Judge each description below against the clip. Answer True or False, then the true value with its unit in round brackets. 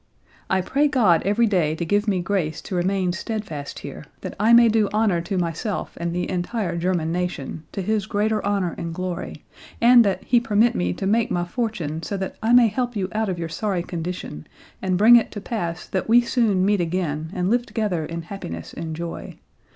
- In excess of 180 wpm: True (205 wpm)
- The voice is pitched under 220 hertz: True (190 Hz)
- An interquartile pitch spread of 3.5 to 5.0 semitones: True (4.2 semitones)